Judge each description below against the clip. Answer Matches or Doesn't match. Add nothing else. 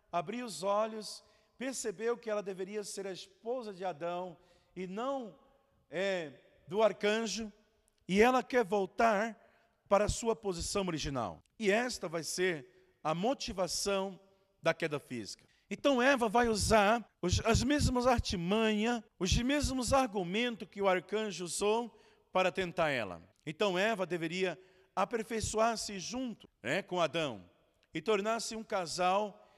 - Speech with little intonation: Doesn't match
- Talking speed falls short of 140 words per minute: Matches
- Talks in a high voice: Matches